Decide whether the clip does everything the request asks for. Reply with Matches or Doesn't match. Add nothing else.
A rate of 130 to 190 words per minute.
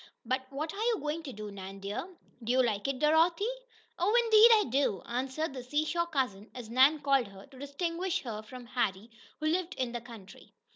Doesn't match